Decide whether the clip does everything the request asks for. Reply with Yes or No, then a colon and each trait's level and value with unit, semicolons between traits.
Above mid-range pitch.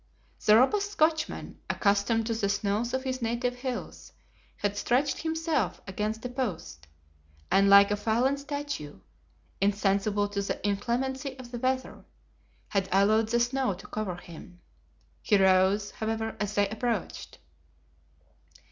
Yes: high, 220 Hz